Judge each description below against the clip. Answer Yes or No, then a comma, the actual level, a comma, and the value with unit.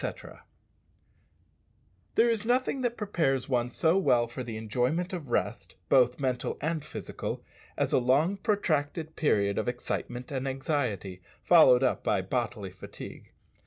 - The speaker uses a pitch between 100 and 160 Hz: Yes, low, 135 Hz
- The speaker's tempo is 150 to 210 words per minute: No, average, 140 wpm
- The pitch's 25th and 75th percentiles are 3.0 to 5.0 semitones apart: No, wide, 5.5 semitones